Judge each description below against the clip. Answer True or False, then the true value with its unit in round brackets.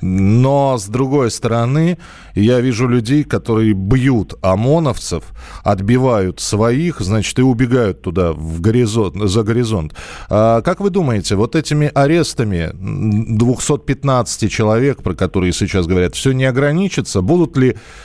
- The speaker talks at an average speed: True (125 wpm)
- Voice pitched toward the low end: True (115 Hz)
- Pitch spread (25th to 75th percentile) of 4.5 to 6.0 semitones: True (5.0 semitones)